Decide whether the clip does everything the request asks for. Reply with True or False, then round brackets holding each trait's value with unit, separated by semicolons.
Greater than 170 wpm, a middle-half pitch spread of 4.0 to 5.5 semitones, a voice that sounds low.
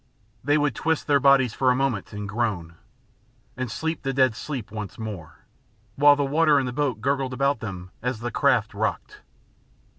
True (180 wpm; 4.7 semitones; 130 Hz)